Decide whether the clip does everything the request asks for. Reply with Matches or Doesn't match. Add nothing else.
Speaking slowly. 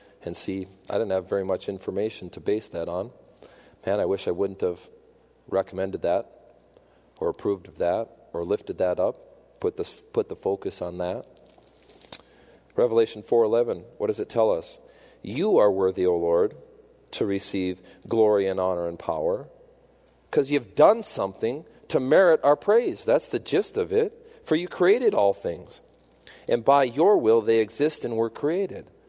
Doesn't match